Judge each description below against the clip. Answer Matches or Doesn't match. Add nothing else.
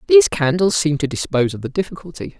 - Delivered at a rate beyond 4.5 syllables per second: Matches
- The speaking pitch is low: Doesn't match